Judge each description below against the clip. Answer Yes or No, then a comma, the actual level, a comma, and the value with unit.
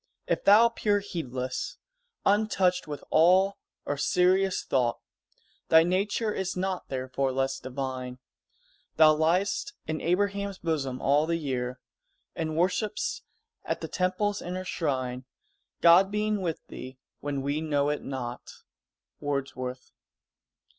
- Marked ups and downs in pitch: Yes, wide, 6.0 semitones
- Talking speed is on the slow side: Yes, slow, 120 wpm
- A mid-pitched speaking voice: Yes, medium, 160 Hz